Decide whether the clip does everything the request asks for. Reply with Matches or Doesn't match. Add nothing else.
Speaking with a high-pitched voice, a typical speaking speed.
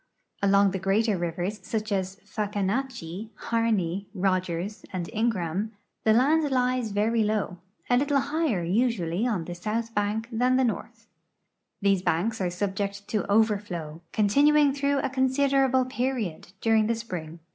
Matches